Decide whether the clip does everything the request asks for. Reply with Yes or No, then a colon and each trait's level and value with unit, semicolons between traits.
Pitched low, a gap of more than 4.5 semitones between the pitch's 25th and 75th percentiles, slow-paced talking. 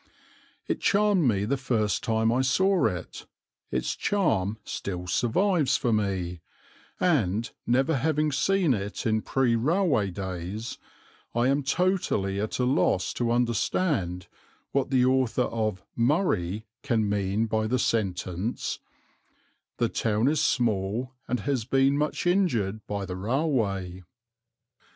Yes: low, 115 Hz; wide, 5.5 semitones; slow, 130 wpm